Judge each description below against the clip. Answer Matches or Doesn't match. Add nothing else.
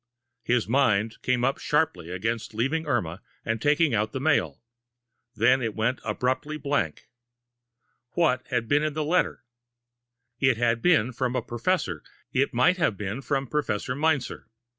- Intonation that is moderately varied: Matches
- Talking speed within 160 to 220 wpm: Doesn't match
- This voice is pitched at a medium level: Doesn't match